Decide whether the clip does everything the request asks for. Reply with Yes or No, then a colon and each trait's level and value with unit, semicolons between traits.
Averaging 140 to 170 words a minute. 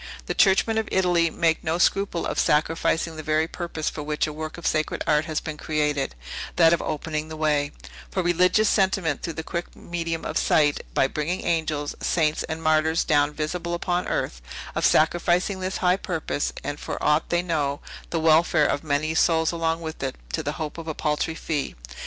No: average, 195 wpm